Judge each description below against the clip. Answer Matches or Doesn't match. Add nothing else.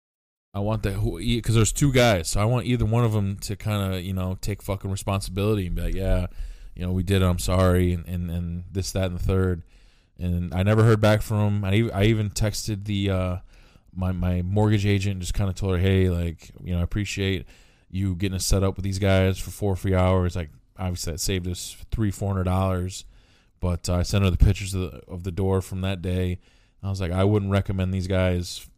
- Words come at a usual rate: Doesn't match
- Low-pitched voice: Matches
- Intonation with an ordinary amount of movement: Doesn't match